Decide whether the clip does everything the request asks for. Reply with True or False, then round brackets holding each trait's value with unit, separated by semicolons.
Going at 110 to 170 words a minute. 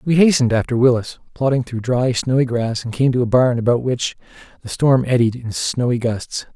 False (200 wpm)